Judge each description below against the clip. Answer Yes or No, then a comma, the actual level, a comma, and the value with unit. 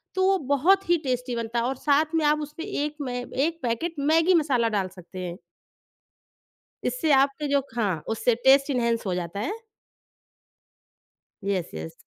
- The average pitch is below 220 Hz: No, very high, 265 Hz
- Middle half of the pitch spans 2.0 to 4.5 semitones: No, average, 5.0 semitones